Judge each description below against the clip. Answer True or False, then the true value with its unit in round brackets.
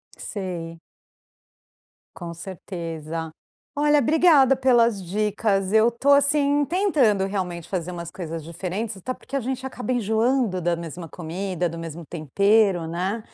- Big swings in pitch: True (6.5 semitones)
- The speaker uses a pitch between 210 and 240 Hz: False (195 Hz)